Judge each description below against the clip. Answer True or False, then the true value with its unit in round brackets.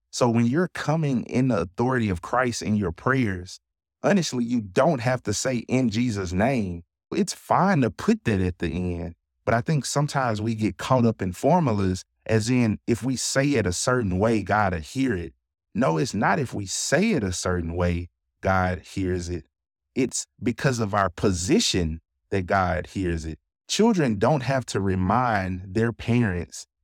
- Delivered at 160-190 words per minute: True (180 wpm)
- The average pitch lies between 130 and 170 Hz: False (105 Hz)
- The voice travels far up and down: True (5.8 semitones)